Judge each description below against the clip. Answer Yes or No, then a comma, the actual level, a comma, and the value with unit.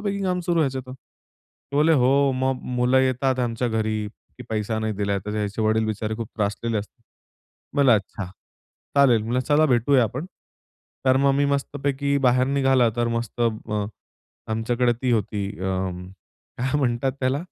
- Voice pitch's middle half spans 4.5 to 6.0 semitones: No, average, 3.7 semitones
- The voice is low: Yes, low, 125 Hz